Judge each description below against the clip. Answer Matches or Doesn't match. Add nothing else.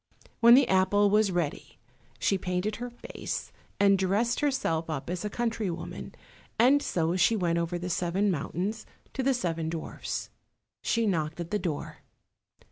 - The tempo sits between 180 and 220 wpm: Doesn't match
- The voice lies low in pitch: Doesn't match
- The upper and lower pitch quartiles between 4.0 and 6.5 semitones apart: Matches